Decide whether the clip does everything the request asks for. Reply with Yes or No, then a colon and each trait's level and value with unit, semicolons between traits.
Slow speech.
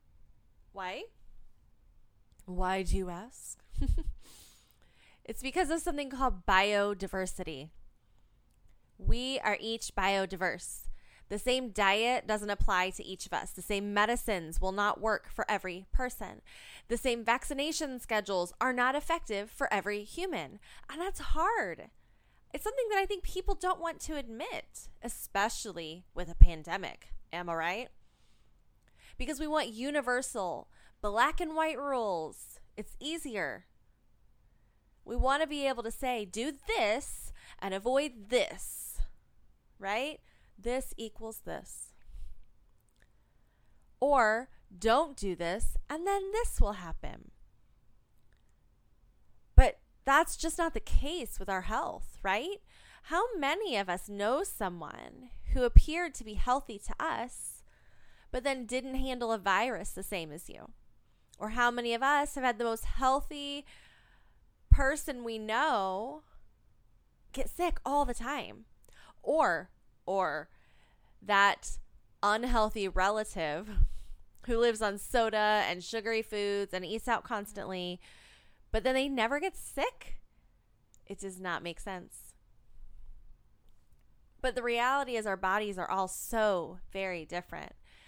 Yes: slow, 125 wpm